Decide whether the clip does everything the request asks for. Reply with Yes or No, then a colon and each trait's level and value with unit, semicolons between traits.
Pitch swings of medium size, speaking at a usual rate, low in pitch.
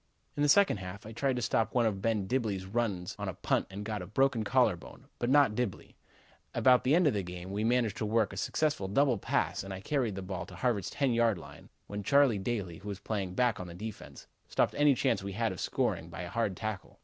No: average, 4.4 semitones; fast, 245 wpm; low, 110 Hz